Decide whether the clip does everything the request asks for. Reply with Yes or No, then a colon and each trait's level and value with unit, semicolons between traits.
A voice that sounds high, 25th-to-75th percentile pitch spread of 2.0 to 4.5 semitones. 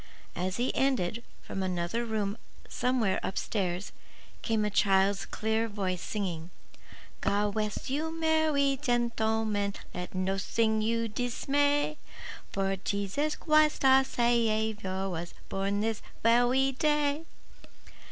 No: high, 220 Hz; average, 5.2 semitones